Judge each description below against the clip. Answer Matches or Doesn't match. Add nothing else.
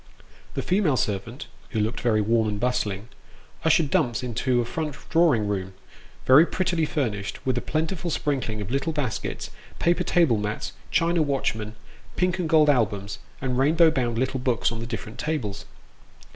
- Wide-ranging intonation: Matches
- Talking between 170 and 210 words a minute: Doesn't match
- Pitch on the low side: Matches